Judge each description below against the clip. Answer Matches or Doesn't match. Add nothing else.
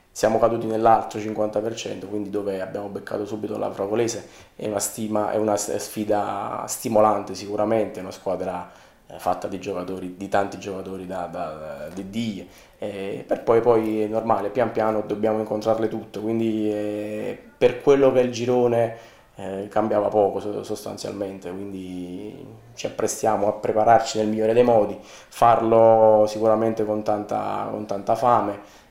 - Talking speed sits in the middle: Matches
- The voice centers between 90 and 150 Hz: Matches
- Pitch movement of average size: Doesn't match